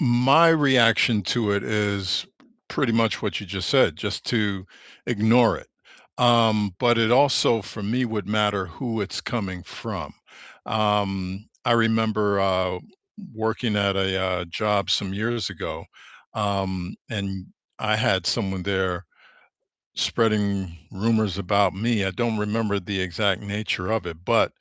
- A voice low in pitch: Yes, low, 105 Hz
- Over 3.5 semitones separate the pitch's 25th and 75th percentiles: No, average, 2.8 semitones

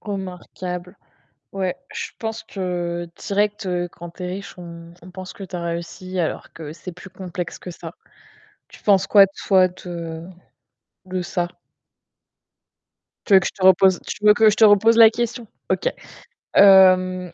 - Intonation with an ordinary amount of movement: No, narrow, 2.2 semitones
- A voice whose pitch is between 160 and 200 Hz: Yes, medium, 185 Hz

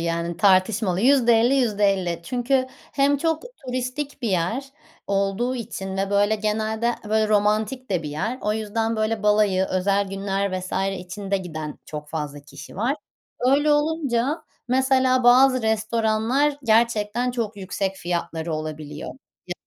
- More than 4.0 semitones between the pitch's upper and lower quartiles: Yes, average, 4.6 semitones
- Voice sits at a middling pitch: No, high, 215 Hz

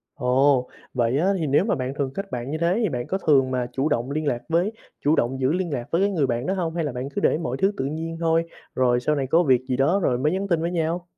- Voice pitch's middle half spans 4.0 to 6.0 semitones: Yes, average, 4.6 semitones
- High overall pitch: No, medium, 145 Hz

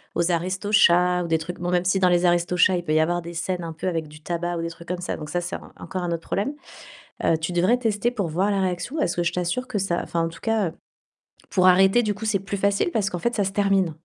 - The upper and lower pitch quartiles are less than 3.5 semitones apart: Yes, narrow, 2.4 semitones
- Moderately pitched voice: Yes, medium, 180 Hz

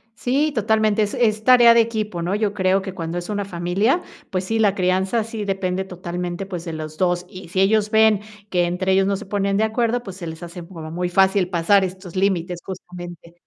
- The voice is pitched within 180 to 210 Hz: Yes, high, 190 Hz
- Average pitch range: Yes, average, 3.2 semitones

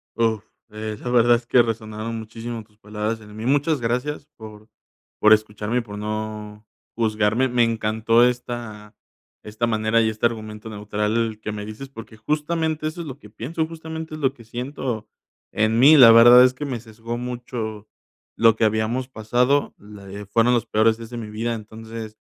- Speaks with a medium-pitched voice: No, low, 115 Hz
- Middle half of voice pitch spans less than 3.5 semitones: Yes, narrow, 2.4 semitones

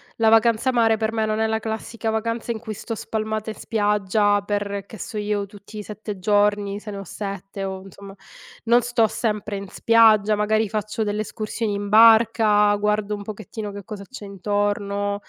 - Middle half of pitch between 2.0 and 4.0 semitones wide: No, narrow, 1.5 semitones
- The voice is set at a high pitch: Yes, high, 210 Hz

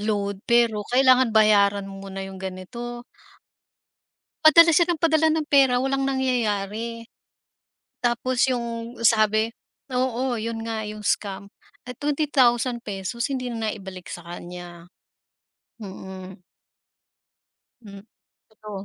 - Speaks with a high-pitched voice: Yes, high, 230 Hz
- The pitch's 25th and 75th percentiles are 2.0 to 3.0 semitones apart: No, average, 4.1 semitones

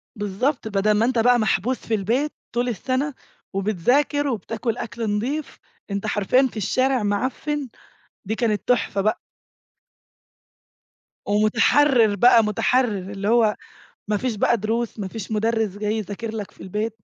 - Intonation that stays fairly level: No, average, 3.1 semitones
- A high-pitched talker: Yes, high, 220 Hz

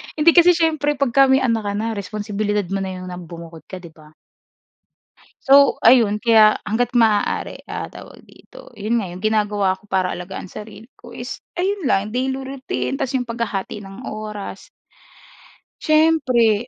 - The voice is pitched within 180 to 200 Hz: No, high, 220 Hz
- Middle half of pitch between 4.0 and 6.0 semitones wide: Yes, average, 4.8 semitones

